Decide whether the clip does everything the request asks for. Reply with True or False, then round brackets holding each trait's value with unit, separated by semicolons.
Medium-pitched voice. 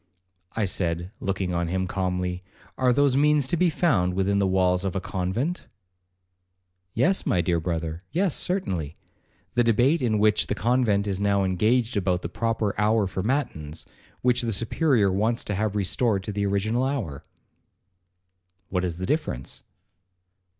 False (100 Hz)